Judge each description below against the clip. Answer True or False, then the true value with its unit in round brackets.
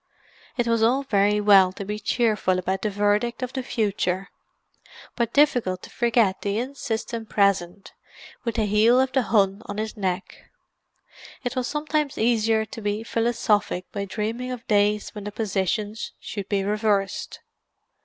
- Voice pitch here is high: True (215 Hz)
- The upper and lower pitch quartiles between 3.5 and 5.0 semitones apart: False (2.8 semitones)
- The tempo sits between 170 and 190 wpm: False (155 wpm)